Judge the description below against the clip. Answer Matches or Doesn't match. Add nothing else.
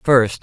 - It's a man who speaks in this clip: Matches